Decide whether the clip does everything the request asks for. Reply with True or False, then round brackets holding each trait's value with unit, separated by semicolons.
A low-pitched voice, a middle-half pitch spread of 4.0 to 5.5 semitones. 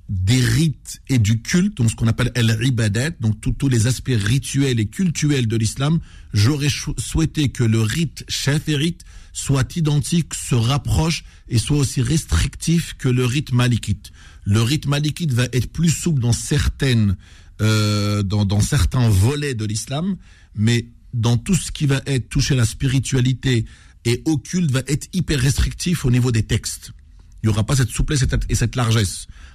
True (125 Hz; 4.7 semitones)